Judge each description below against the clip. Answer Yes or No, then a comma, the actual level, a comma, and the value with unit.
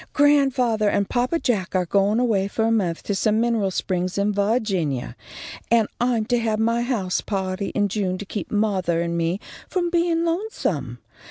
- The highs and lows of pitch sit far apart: No, average, 4.2 semitones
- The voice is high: Yes, high, 210 Hz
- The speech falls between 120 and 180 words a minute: Yes, average, 175 wpm